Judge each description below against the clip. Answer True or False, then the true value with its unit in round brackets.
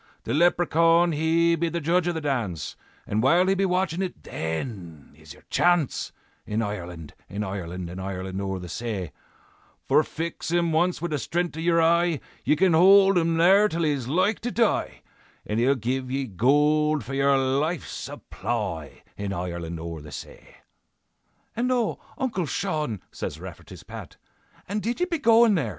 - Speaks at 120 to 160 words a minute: False (170 wpm)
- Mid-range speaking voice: True (150 Hz)